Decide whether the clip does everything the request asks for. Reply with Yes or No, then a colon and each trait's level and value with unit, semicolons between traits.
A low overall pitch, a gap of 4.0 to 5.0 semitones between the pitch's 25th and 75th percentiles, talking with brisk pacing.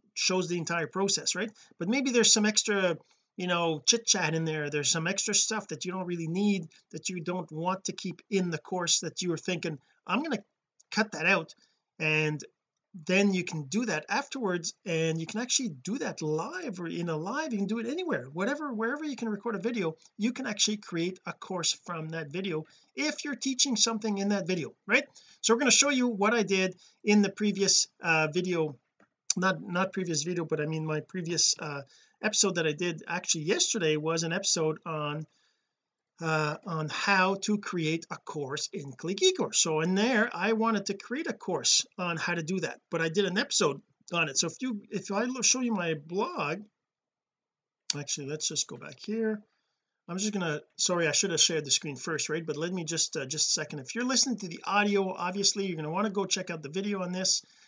No: medium, 185 Hz; average, 4.7 semitones; fast, 215 wpm